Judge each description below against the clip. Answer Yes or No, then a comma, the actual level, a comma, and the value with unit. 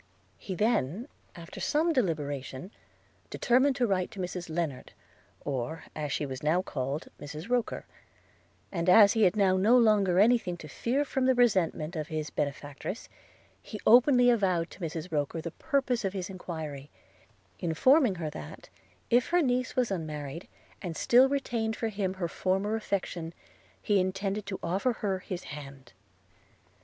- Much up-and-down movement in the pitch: Yes, wide, 6.5 semitones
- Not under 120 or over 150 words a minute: No, average, 160 wpm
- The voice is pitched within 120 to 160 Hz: No, medium, 185 Hz